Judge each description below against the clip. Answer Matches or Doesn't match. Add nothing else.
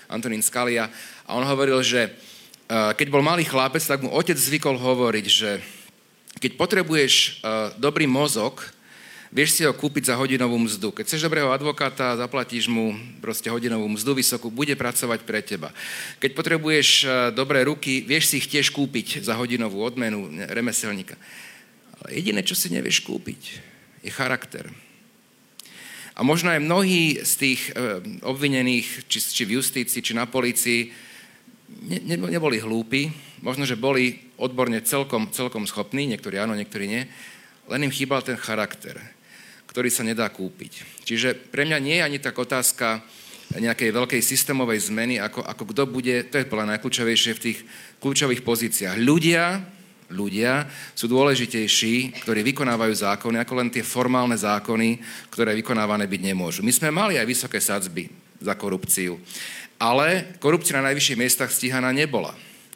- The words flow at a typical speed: Matches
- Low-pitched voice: Matches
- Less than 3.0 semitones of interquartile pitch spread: Doesn't match